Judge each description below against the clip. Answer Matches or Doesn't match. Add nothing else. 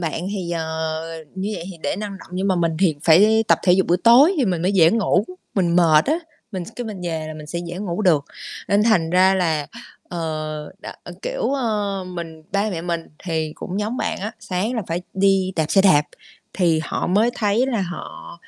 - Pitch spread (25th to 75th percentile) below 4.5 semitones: Matches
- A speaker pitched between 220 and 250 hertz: Doesn't match